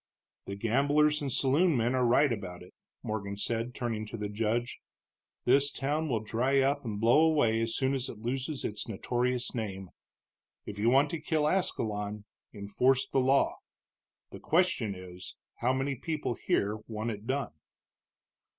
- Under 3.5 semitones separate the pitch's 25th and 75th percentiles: No, average, 4.4 semitones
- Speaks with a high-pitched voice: No, low, 120 Hz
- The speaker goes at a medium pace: Yes, average, 160 wpm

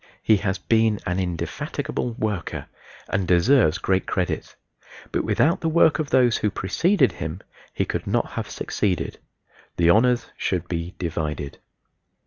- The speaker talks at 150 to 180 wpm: No, average, 140 wpm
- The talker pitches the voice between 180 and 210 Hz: No, very low, 95 Hz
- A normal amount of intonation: No, wide, 5.8 semitones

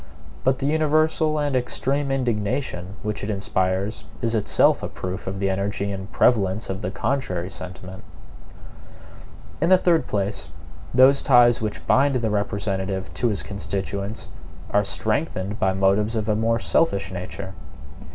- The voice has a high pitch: No, low, 105 Hz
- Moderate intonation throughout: Yes, average, 4.8 semitones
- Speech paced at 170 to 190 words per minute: No, average, 145 wpm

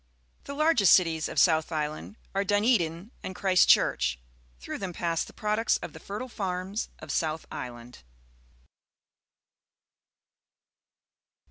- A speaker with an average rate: No, slow, 115 wpm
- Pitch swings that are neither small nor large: Yes, average, 4.7 semitones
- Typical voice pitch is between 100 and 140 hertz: No, medium, 180 Hz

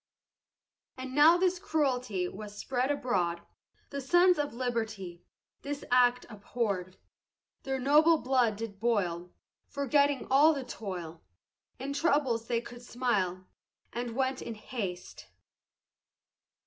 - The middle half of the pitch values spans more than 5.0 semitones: Yes, wide, 5.4 semitones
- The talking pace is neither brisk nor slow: No, slow, 115 wpm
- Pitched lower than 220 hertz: No, high, 245 Hz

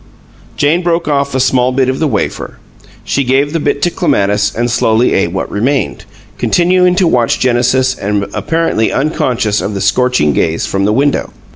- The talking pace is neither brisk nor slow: Yes, average, 175 wpm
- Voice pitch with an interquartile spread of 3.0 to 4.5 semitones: No, average, 5.1 semitones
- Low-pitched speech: Yes, low, 130 Hz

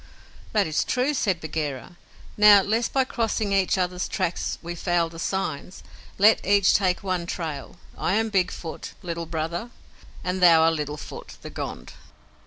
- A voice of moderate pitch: Yes, medium, 180 Hz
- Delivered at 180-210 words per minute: No, average, 165 wpm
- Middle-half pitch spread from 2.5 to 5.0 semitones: Yes, average, 3.5 semitones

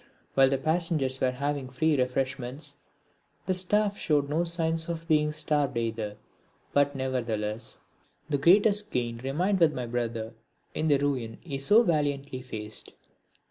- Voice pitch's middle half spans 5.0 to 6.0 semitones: No, average, 4.2 semitones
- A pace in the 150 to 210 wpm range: No, average, 140 wpm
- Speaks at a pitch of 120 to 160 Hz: Yes, medium, 140 Hz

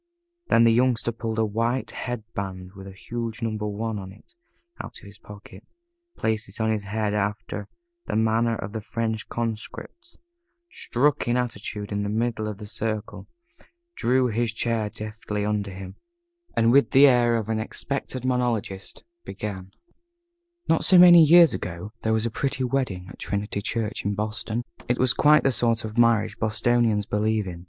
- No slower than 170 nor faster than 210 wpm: Yes, average, 175 wpm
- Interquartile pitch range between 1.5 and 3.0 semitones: Yes, narrow, 2.5 semitones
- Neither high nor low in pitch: No, low, 110 Hz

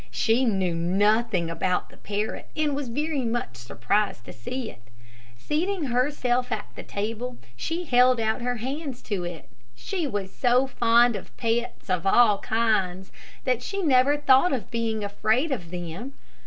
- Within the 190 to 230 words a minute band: No, average, 160 wpm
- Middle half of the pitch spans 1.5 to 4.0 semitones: No, average, 4.8 semitones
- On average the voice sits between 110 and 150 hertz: No, high, 230 Hz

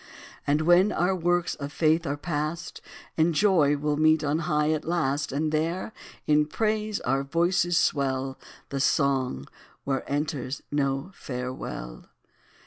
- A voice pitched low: No, medium, 150 Hz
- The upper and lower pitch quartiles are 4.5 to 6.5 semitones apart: No, average, 3.5 semitones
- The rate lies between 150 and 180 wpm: No, average, 140 wpm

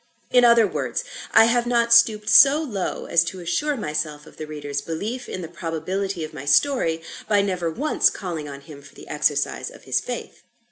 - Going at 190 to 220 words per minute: Yes, average, 195 wpm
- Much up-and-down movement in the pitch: Yes, wide, 7.2 semitones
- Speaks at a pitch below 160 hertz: No, medium, 180 Hz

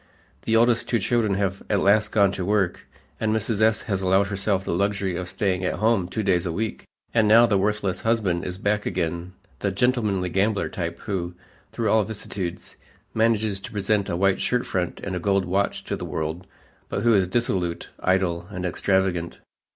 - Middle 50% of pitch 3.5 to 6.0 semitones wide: No, average, 2.9 semitones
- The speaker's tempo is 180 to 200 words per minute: Yes, average, 190 wpm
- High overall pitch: No, low, 100 Hz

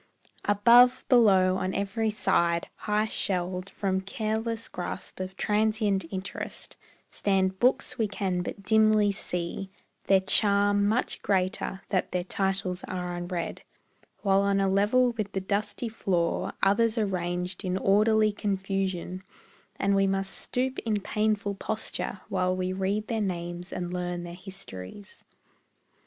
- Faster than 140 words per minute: No, slow, 135 wpm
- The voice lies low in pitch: No, high, 195 Hz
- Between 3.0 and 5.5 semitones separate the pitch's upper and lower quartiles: No, narrow, 2.4 semitones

